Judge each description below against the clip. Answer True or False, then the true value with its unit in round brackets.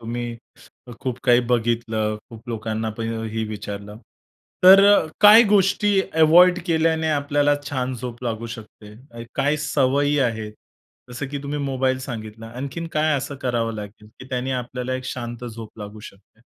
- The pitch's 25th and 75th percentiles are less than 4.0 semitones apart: False (4.4 semitones)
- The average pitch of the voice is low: True (125 Hz)